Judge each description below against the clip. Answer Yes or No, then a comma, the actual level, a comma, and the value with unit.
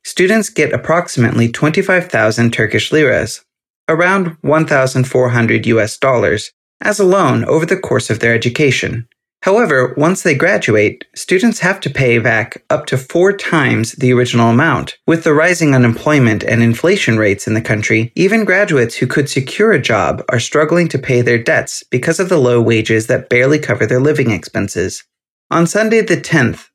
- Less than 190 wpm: Yes, average, 165 wpm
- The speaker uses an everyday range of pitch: No, wide, 6.0 semitones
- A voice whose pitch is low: Yes, low, 130 Hz